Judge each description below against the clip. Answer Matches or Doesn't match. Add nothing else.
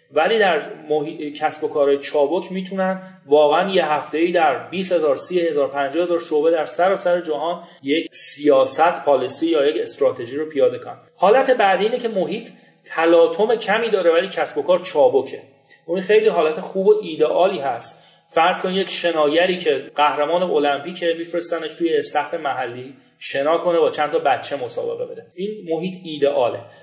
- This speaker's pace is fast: Matches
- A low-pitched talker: Doesn't match